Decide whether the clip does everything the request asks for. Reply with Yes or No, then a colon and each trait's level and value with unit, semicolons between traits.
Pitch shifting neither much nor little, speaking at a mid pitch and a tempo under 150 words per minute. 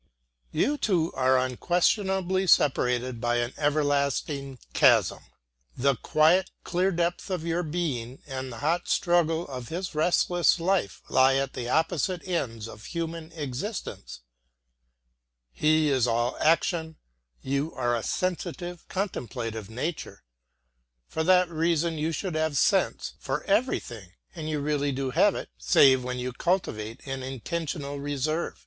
Yes: average, 5.0 semitones; medium, 150 Hz; slow, 135 wpm